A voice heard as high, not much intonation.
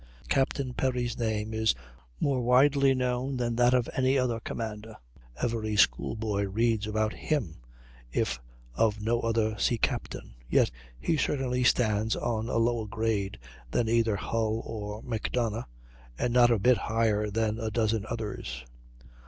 No: low, 115 Hz; narrow, 2.3 semitones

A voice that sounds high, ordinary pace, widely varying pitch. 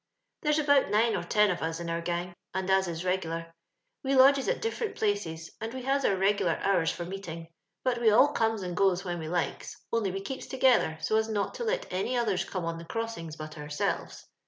No: high, 195 Hz; fast, 225 wpm; wide, 5.7 semitones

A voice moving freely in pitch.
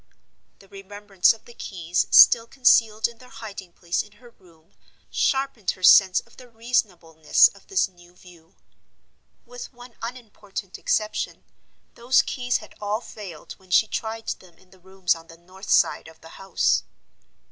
No: average, 4.5 semitones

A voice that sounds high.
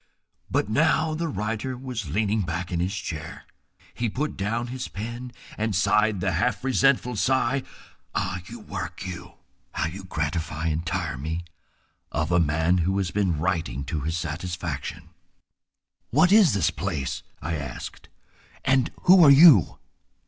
No: very low, 95 Hz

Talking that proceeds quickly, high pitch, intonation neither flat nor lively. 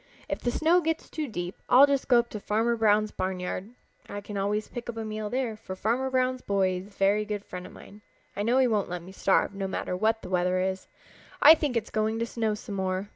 Yes: fast, 250 wpm; high, 215 Hz; average, 3.7 semitones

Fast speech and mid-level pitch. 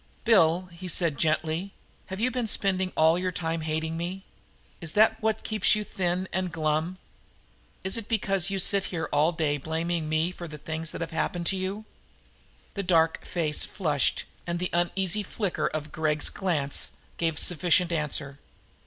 No: average, 170 wpm; medium, 175 Hz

